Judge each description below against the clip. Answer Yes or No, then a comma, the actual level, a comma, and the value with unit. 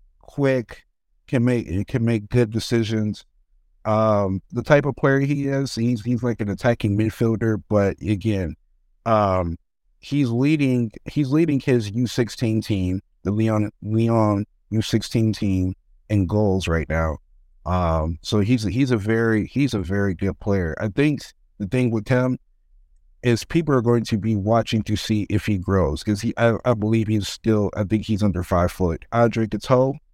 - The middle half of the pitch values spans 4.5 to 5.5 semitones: No, average, 4.0 semitones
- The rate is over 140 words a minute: Yes, average, 170 wpm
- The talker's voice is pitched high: No, low, 110 Hz